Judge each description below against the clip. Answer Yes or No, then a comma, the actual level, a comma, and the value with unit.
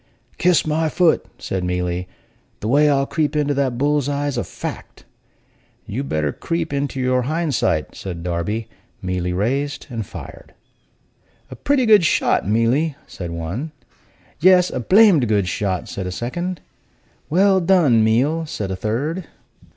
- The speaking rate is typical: Yes, average, 150 wpm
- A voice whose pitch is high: No, low, 135 Hz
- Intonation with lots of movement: Yes, wide, 8.1 semitones